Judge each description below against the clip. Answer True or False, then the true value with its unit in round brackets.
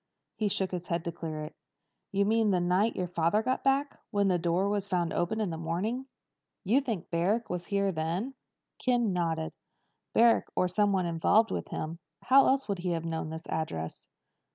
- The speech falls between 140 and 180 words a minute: False (190 wpm)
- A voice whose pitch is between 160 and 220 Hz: True (185 Hz)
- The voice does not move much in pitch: False (4.4 semitones)